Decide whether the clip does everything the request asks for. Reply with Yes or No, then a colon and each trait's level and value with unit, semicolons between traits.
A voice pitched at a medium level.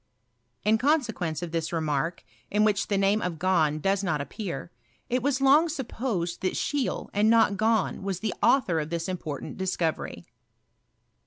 No: high, 195 Hz